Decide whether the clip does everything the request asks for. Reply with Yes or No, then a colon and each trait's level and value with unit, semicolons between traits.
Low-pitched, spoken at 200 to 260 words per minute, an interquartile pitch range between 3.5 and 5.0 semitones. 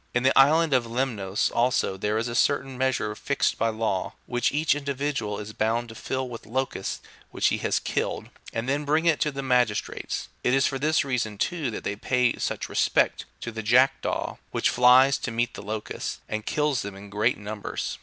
Yes: low, 125 Hz; fast, 205 wpm; average, 3.8 semitones